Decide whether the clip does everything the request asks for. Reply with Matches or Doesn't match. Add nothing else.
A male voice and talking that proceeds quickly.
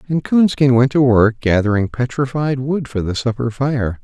Doesn't match